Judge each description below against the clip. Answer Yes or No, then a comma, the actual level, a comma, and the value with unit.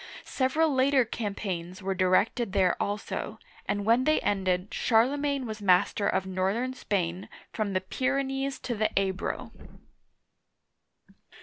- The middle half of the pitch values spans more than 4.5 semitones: Yes, wide, 5.4 semitones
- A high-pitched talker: Yes, high, 210 Hz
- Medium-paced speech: No, slow, 120 wpm